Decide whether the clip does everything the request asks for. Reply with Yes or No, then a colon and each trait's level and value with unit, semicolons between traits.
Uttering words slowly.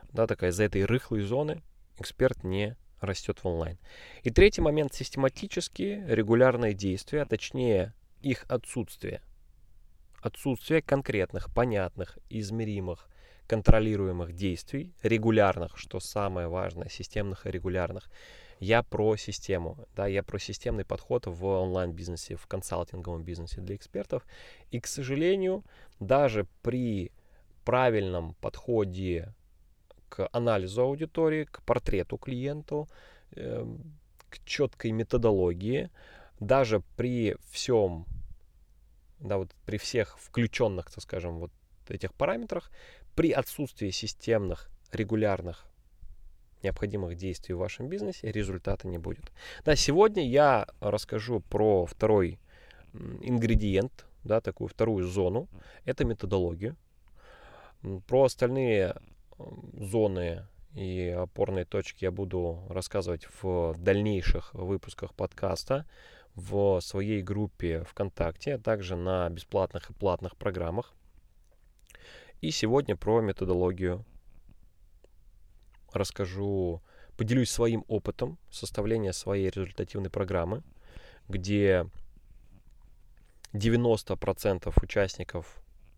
Yes: slow, 100 wpm